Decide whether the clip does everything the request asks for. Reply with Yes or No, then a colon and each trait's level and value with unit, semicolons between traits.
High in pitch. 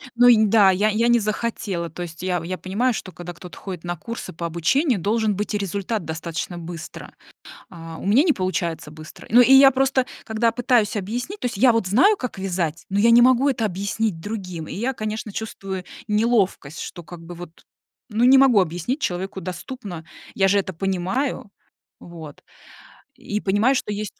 Yes: high, 200 Hz